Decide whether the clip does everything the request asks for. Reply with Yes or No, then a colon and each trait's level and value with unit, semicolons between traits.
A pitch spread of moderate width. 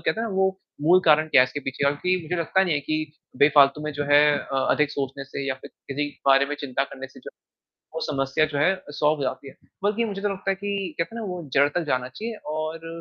Yes: average, 4.9 semitones